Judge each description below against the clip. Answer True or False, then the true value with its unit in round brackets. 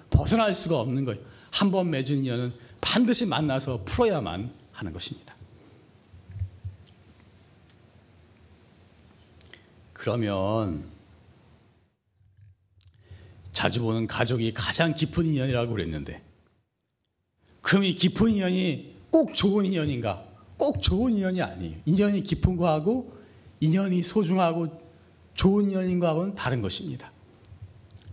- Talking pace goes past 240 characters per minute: False (235 characters per minute)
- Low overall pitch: True (115 Hz)